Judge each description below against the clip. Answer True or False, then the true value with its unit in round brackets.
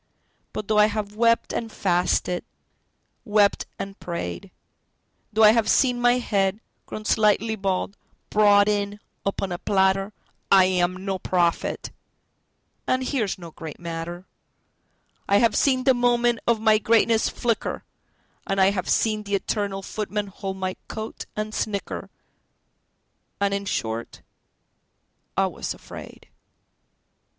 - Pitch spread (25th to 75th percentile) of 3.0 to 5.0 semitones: False (2.4 semitones)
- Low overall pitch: False (205 Hz)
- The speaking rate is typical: False (120 wpm)